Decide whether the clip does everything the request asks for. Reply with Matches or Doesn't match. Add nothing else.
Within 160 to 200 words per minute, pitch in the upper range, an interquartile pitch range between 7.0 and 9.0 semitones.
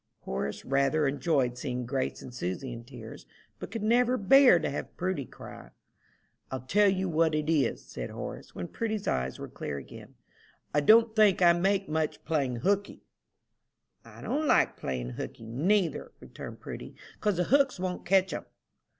Doesn't match